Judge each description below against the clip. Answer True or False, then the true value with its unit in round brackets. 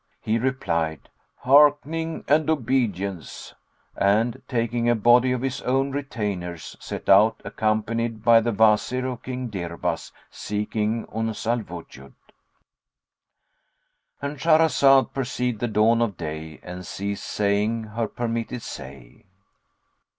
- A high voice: False (115 Hz)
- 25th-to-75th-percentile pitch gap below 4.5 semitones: True (4.0 semitones)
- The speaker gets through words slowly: True (115 wpm)